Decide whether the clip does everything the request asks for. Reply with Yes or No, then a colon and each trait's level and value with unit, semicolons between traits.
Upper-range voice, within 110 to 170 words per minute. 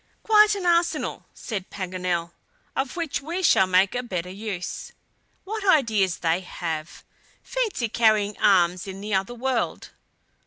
Yes: high, 210 Hz; average, 140 wpm